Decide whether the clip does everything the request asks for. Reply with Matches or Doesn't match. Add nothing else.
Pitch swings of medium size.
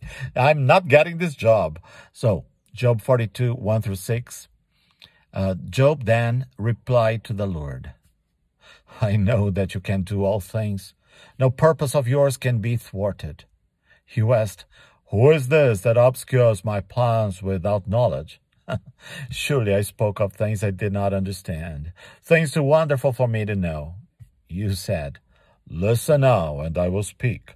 Matches